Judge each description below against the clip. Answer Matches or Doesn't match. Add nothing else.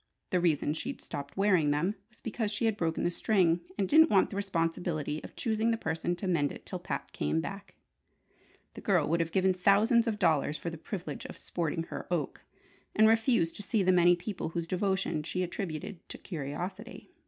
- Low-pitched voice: Doesn't match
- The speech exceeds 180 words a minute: Matches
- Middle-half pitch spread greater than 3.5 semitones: Matches